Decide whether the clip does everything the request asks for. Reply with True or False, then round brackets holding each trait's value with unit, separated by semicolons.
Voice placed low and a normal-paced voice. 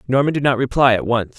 False (125 Hz; 260 wpm)